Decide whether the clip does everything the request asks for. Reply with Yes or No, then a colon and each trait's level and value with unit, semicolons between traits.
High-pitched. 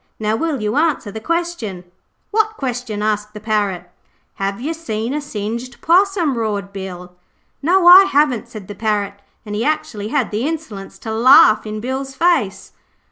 Yes: high, 230 Hz